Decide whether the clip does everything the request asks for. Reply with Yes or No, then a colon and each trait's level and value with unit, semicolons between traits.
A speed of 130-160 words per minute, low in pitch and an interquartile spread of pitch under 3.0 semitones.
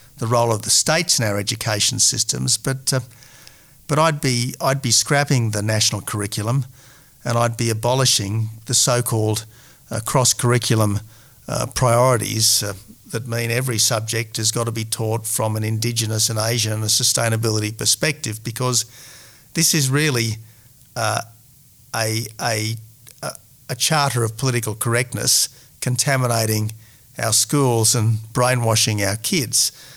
Yes: slow, 135 wpm; low, 120 Hz; narrow, 2.5 semitones